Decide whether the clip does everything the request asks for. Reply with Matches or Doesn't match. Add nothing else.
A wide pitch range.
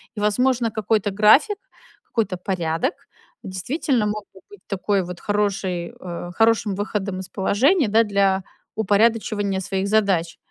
Doesn't match